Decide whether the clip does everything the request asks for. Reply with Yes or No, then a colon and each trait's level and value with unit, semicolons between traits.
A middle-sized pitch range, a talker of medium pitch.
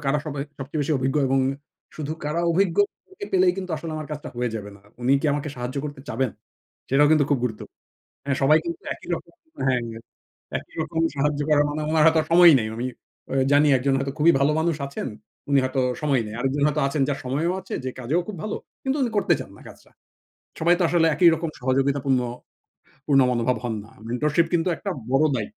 Yes: average, 3.5 semitones; medium, 145 Hz